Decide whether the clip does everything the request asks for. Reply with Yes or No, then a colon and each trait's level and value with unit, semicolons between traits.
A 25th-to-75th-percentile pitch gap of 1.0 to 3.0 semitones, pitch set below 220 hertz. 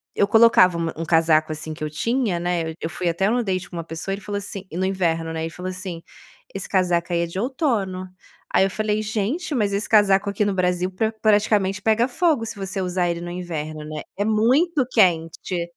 No: average, 3.9 semitones; high, 190 Hz